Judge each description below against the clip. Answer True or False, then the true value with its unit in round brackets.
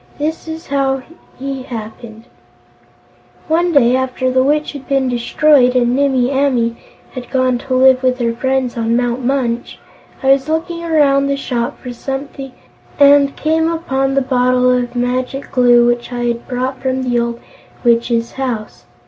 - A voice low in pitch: False (260 Hz)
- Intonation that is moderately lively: False (2.2 semitones)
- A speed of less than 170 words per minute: True (160 wpm)